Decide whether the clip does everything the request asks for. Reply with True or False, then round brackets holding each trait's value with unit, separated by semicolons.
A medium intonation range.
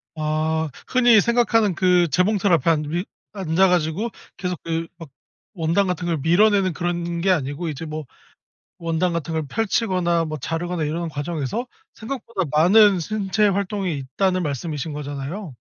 True (3.6 semitones)